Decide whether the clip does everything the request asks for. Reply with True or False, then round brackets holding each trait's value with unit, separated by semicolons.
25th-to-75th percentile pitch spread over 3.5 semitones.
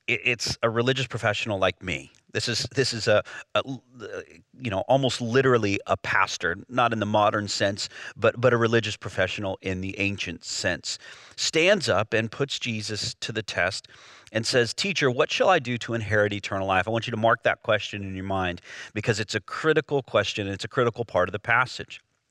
False (3.1 semitones)